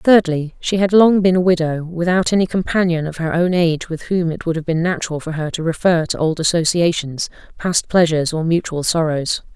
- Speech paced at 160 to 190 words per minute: No, fast, 205 wpm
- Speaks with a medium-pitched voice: Yes, medium, 170 Hz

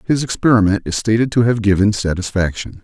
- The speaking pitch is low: Yes, low, 105 Hz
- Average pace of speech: Yes, average, 170 wpm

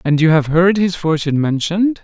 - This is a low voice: No, medium, 170 Hz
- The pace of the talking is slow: No, fast, 205 wpm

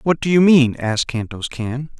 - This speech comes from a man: Yes, male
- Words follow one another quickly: Yes, fast, 210 wpm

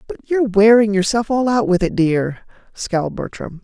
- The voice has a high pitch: Yes, high, 210 Hz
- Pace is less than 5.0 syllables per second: No, 5.1 syllables/s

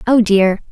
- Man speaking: No, female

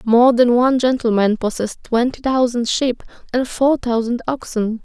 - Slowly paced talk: No, average, 150 wpm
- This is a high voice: Yes, high, 240 Hz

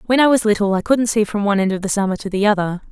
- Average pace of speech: No, fast, 330 wpm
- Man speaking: No, female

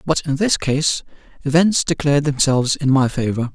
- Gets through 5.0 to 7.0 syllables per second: Yes, 5.3 syllables/s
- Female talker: No, male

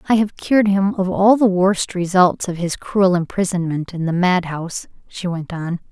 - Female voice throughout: Yes, female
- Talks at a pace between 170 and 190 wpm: No, fast, 205 wpm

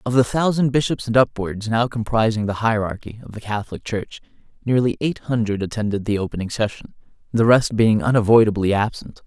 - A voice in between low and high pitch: No, low, 115 Hz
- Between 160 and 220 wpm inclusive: Yes, average, 170 wpm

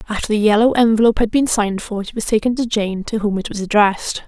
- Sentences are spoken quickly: Yes, fast, 255 wpm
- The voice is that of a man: No, female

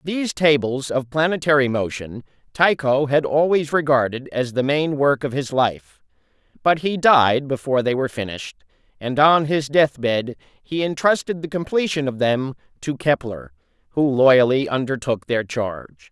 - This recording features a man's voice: Yes, male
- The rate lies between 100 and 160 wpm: Yes, average, 155 wpm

